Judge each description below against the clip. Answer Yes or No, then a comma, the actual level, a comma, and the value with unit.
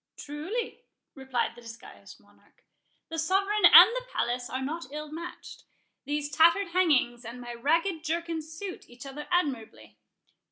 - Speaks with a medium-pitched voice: No, very high, 305 Hz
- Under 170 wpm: Yes, slow, 135 wpm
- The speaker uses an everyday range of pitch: Yes, average, 5.0 semitones